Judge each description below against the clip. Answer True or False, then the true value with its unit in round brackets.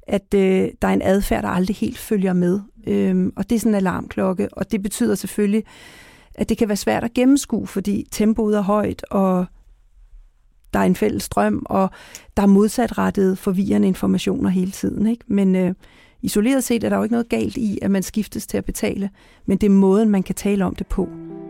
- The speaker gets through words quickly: False (210 wpm)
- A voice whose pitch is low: False (200 Hz)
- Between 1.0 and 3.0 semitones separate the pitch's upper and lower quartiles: True (2.5 semitones)